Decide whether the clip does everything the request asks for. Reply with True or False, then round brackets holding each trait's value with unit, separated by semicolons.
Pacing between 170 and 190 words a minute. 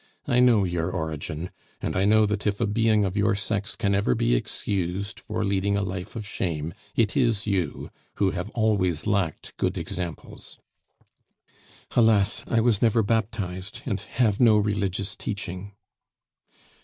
False (155 wpm)